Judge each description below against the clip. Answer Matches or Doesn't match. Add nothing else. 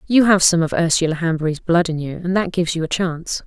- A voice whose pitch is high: Doesn't match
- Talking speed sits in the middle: Doesn't match